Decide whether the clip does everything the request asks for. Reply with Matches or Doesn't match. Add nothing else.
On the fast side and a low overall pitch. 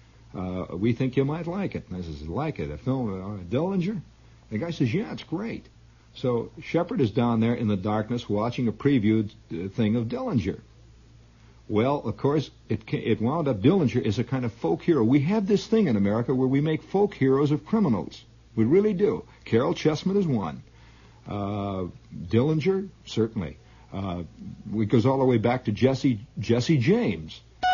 Doesn't match